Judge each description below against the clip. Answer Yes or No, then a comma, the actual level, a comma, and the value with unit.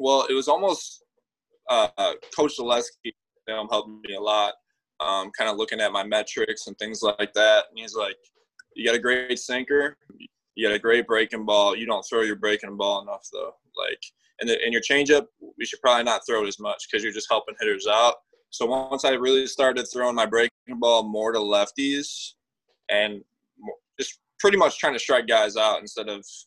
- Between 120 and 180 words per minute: No, average, 195 wpm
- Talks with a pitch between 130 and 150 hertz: Yes, low, 135 Hz